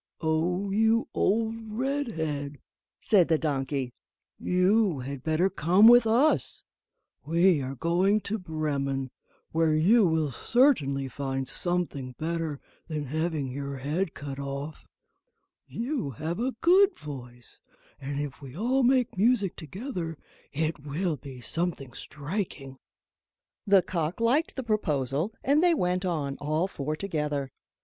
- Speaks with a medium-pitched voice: Yes, medium, 160 Hz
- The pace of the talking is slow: Yes, slow, 130 wpm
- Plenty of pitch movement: Yes, wide, 6.3 semitones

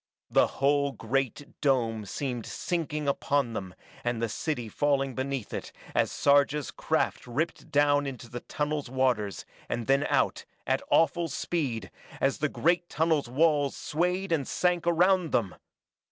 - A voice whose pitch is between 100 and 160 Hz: Yes, medium, 140 Hz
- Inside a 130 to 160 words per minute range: Yes, average, 145 wpm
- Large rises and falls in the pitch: No, average, 4.2 semitones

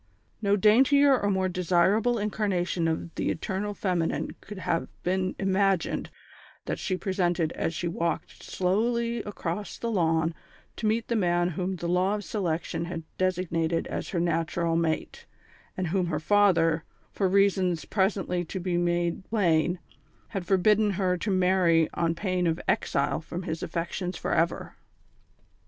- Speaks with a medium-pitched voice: Yes, medium, 180 Hz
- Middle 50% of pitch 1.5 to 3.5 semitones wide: Yes, average, 2.9 semitones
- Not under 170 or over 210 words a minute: No, average, 150 wpm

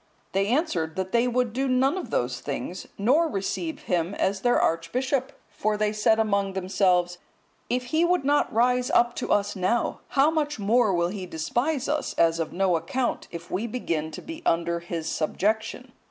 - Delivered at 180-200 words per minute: Yes, average, 185 wpm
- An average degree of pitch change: No, wide, 6.1 semitones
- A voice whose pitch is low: No, high, 210 Hz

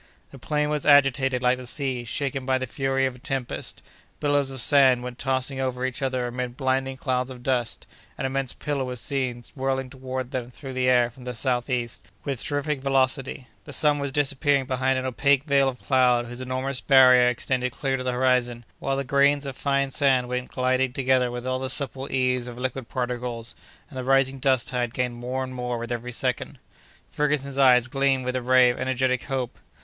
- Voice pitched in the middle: No, low, 130 Hz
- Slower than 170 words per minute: No, average, 200 wpm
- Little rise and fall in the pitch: Yes, narrow, 1.4 semitones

